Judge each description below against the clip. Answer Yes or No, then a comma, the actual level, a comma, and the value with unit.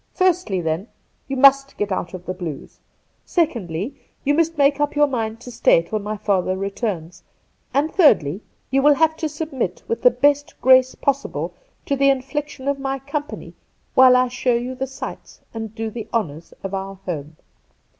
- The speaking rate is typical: Yes, average, 175 wpm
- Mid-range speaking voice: No, very high, 250 Hz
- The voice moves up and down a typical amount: No, wide, 6.2 semitones